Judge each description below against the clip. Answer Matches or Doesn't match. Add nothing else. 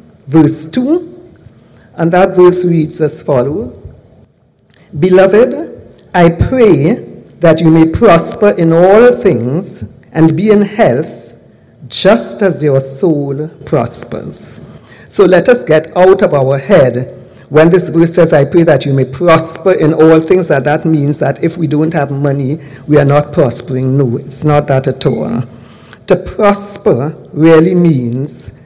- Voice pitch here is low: Doesn't match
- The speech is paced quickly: Doesn't match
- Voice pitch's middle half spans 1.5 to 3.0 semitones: Doesn't match